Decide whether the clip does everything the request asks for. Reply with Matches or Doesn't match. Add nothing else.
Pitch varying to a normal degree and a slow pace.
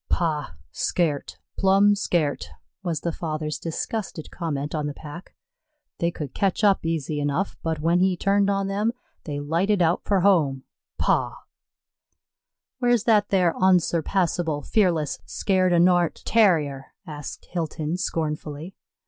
Matches